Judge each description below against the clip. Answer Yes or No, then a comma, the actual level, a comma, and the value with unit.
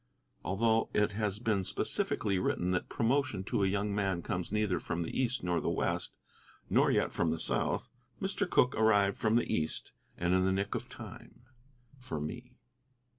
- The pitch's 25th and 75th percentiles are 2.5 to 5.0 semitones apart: Yes, average, 3.5 semitones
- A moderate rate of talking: Yes, average, 180 wpm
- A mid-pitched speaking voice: No, low, 100 Hz